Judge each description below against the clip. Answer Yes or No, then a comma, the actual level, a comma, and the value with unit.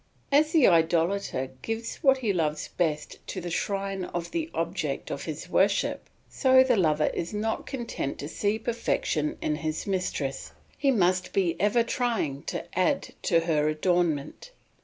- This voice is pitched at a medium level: Yes, medium, 180 Hz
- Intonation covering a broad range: Yes, wide, 6.1 semitones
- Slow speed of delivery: No, average, 160 wpm